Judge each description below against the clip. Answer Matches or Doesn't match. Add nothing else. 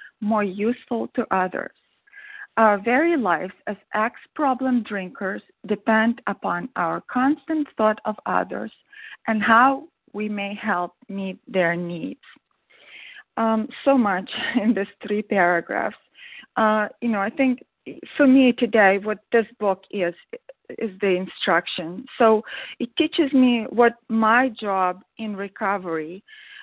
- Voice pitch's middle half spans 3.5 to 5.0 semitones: Matches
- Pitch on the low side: Doesn't match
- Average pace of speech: Doesn't match